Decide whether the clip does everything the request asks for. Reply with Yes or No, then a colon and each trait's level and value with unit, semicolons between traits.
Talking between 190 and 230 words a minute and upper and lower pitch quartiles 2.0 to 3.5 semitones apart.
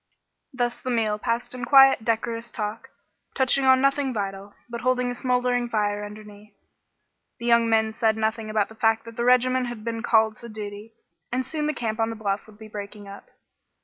Yes: average, 195 wpm; narrow, 2.5 semitones